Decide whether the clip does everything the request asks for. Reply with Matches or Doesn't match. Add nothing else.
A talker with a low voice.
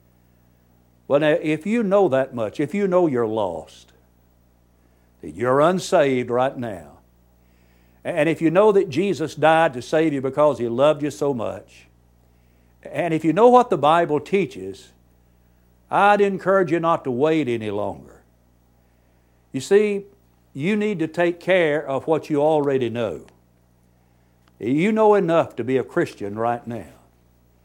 Matches